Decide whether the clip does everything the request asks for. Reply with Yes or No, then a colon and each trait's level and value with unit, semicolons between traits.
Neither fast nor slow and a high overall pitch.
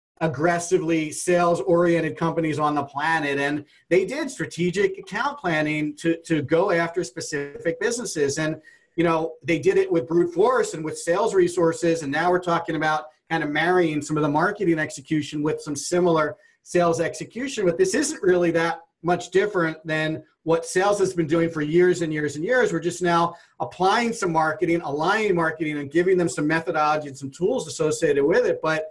No: average, 185 wpm; medium, 165 Hz